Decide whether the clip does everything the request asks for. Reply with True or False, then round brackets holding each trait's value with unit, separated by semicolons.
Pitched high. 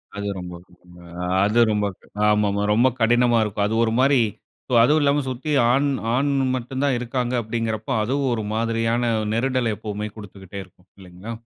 False (115 Hz)